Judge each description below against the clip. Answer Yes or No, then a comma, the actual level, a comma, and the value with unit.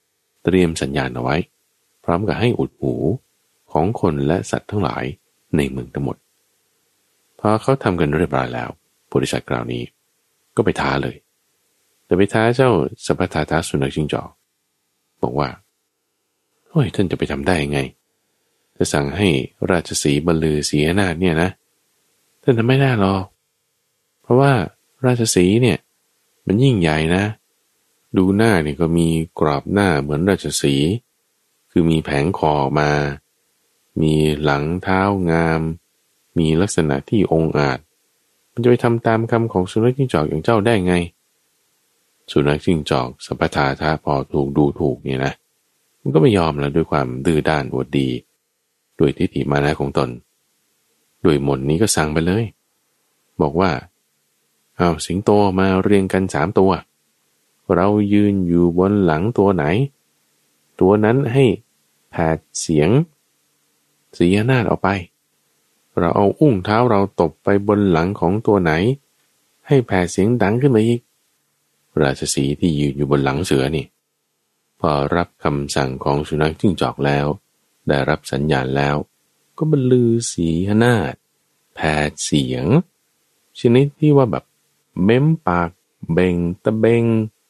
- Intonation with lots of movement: Yes, wide, 6.0 semitones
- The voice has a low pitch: Yes, very low, 85 Hz